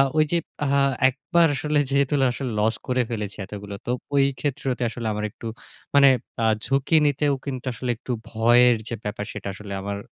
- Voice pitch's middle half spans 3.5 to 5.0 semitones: Yes, average, 4.6 semitones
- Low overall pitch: Yes, low, 125 Hz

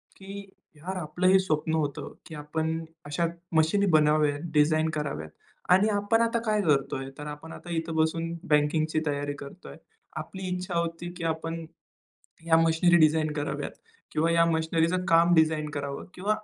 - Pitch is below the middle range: No, medium, 160 Hz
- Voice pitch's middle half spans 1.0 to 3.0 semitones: Yes, narrow, 2.4 semitones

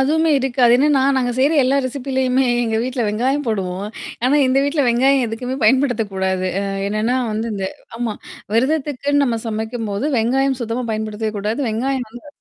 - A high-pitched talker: Yes, high, 245 Hz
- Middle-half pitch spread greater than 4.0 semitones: No, average, 3.5 semitones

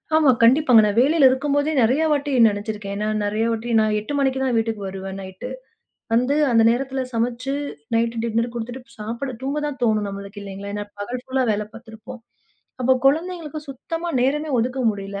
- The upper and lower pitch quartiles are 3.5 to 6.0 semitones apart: Yes, average, 4.2 semitones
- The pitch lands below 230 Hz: No, high, 235 Hz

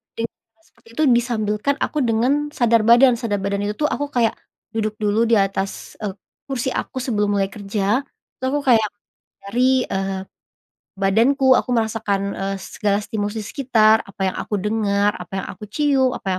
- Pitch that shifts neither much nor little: Yes, average, 3.5 semitones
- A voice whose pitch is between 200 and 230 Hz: Yes, high, 220 Hz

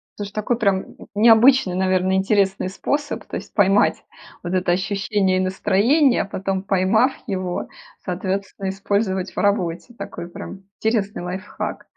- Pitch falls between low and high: No, high, 195 Hz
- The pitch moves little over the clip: Yes, narrow, 2.1 semitones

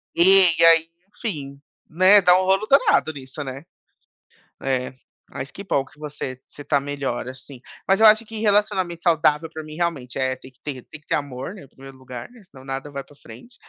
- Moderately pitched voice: Yes, medium, 150 Hz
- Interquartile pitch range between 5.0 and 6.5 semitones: Yes, wide, 5.6 semitones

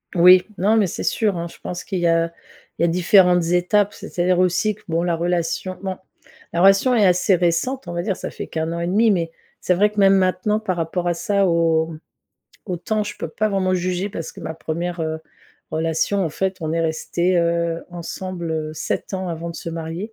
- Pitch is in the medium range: Yes, medium, 175 Hz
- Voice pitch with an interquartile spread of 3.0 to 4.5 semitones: No, narrow, 2.5 semitones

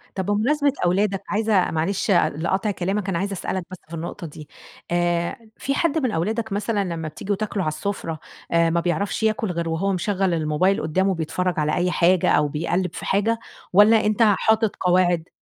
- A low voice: No, medium, 185 Hz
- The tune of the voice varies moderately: Yes, average, 3.5 semitones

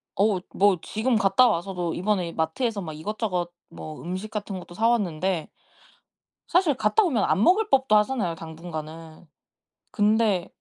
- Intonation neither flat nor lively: Yes, average, 4.3 semitones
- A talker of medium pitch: No, high, 195 Hz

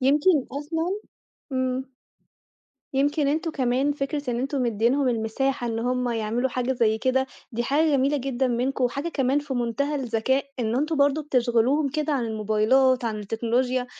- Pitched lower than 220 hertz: No, very high, 260 Hz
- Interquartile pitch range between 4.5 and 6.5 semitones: No, average, 3.0 semitones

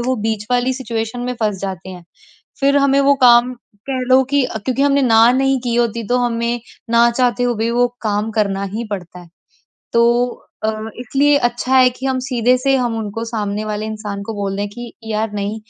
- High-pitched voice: Yes, high, 235 Hz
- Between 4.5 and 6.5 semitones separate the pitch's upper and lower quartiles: No, average, 2.9 semitones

